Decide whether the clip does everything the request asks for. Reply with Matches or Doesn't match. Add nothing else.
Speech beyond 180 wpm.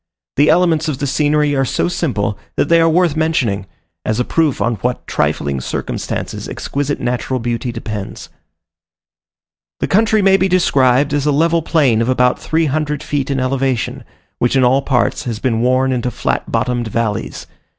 Doesn't match